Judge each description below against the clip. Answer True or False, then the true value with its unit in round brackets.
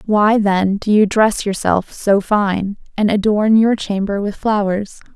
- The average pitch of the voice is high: True (205 Hz)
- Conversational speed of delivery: True (165 wpm)